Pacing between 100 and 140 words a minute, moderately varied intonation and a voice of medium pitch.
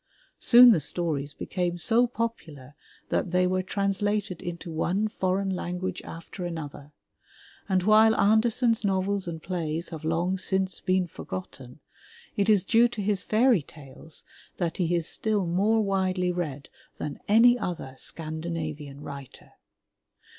Yes: slow, 135 wpm; average, 4.0 semitones; medium, 180 Hz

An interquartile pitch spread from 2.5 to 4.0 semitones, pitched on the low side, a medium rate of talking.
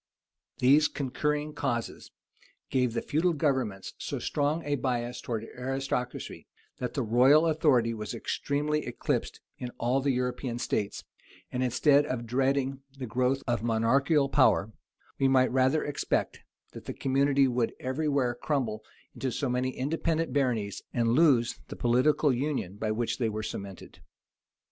Yes: average, 3.1 semitones; low, 130 Hz; average, 145 wpm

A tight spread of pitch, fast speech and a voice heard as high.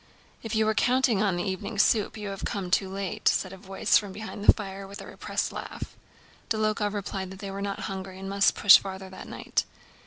Yes: narrow, 1.7 semitones; fast, 225 wpm; high, 200 Hz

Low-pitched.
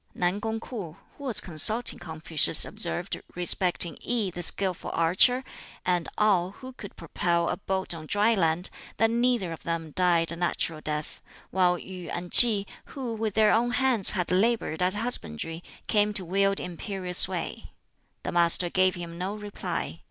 No: medium, 185 Hz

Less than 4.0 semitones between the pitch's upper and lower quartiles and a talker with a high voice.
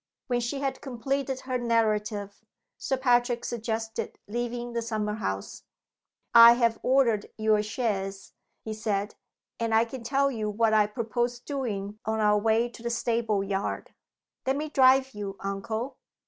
Yes: narrow, 2.6 semitones; high, 230 Hz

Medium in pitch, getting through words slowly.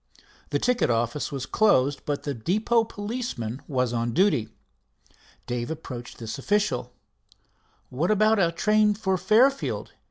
Yes: medium, 165 Hz; slow, 130 wpm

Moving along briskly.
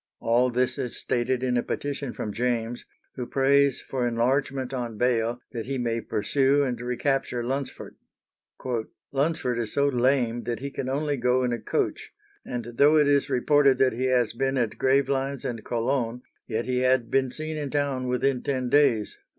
No: average, 175 wpm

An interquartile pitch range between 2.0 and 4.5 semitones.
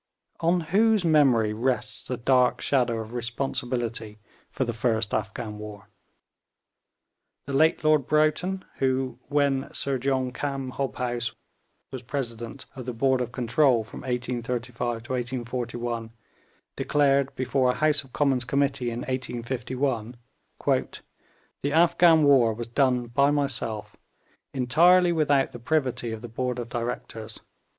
Yes: average, 2.9 semitones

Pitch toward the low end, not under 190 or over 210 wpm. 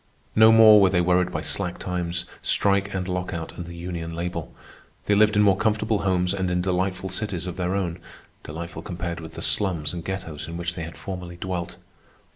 Yes: very low, 90 Hz; average, 195 wpm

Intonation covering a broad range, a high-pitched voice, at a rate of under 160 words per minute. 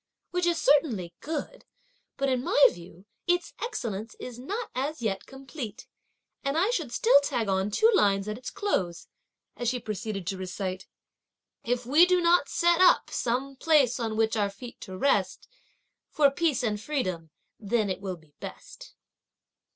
No: wide, 7.1 semitones; high, 245 Hz; average, 165 wpm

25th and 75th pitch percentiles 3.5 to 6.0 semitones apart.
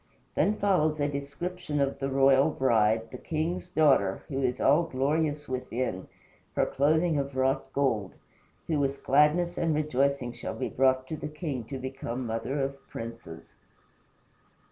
No: average, 2.9 semitones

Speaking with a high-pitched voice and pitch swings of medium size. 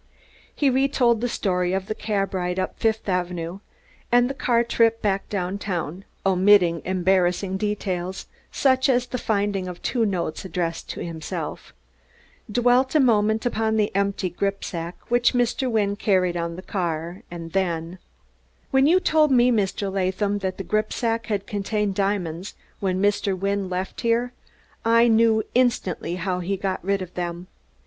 Yes: high, 200 Hz; average, 3.9 semitones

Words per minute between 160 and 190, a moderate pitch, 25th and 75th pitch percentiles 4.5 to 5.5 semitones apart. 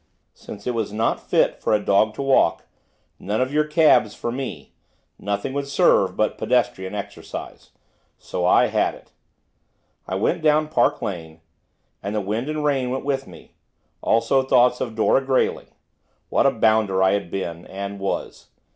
No: average, 165 wpm; low, 115 Hz; average, 5.1 semitones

